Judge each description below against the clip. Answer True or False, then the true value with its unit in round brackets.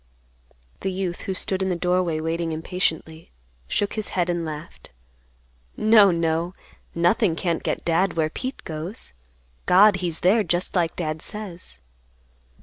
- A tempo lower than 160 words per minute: True (145 wpm)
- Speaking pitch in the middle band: True (175 Hz)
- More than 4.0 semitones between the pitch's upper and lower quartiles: False (2.7 semitones)